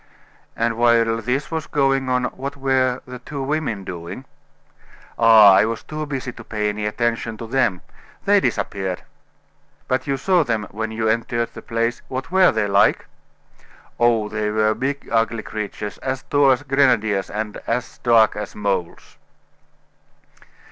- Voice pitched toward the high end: No, low, 115 Hz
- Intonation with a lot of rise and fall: No, average, 3.6 semitones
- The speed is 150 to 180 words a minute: Yes, average, 155 wpm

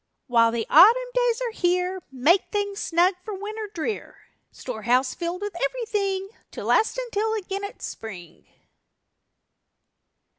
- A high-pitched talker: Yes, very high, 390 Hz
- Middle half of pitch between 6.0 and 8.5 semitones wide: No, wide, 5.6 semitones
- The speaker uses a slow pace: Yes, slow, 125 wpm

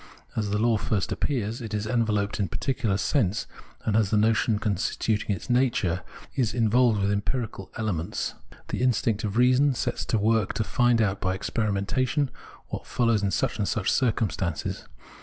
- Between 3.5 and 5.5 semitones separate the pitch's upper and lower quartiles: No, narrow, 2.5 semitones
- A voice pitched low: Yes, low, 110 Hz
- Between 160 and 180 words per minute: Yes, average, 165 wpm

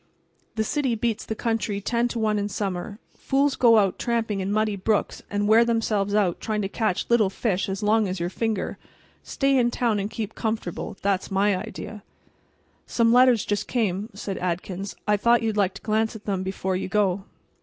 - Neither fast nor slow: Yes, average, 195 wpm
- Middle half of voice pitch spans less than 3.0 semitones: Yes, narrow, 2.5 semitones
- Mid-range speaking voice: No, high, 210 Hz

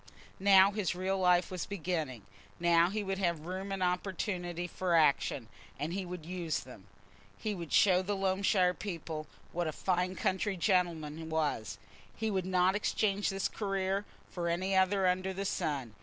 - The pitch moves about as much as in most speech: No, narrow, 2.3 semitones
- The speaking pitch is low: No, medium, 180 Hz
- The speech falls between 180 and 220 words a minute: No, average, 165 wpm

